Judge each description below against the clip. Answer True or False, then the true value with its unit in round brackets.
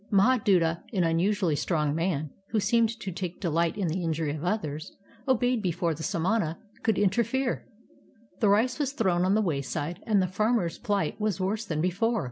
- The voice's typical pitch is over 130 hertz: True (185 Hz)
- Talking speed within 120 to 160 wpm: False (185 wpm)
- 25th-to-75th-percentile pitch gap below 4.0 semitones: False (4.7 semitones)